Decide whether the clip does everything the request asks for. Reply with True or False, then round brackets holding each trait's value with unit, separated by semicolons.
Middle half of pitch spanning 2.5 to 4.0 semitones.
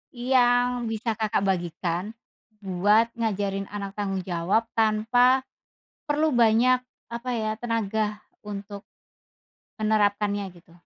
True (2.9 semitones)